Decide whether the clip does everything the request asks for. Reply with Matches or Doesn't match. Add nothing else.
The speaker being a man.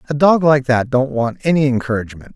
Matches